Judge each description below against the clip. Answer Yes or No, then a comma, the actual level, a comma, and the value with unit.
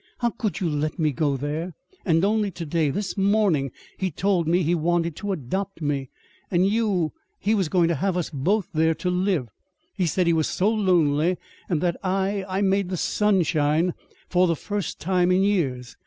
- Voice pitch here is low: No, medium, 180 Hz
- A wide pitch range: No, average, 3.8 semitones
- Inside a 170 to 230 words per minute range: Yes, average, 200 wpm